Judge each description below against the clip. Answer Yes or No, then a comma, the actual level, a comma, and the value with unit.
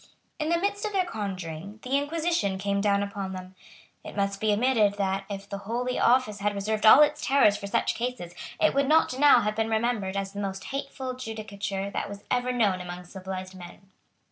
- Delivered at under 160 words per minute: No, average, 200 wpm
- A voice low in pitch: No, high, 205 Hz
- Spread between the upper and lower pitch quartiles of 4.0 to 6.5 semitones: Yes, average, 4.4 semitones